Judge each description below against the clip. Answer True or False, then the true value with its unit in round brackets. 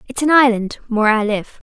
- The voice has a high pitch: True (230 Hz)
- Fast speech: True (210 wpm)